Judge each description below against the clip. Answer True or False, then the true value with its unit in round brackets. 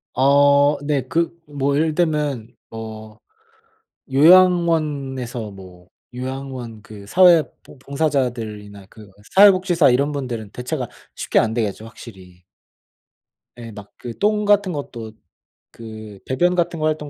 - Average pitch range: False (5.9 semitones)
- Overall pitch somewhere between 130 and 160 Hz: True (135 Hz)